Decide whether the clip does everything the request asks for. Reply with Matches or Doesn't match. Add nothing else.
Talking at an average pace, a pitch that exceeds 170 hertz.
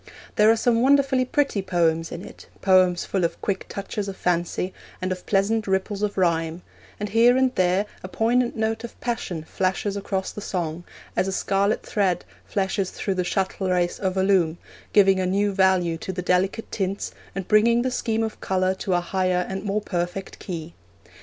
Matches